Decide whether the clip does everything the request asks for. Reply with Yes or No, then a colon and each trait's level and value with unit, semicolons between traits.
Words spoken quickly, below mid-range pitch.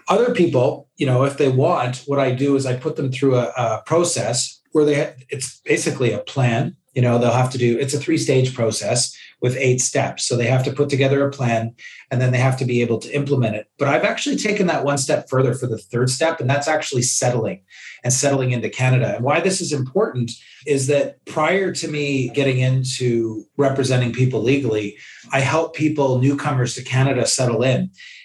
Yes: fast, 210 wpm; low, 130 Hz